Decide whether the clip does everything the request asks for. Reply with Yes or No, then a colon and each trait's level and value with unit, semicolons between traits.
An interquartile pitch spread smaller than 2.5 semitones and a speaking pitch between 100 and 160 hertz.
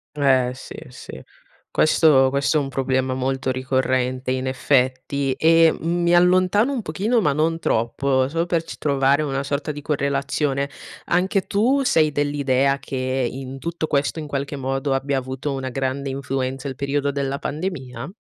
No: average, 2.8 semitones; medium, 140 Hz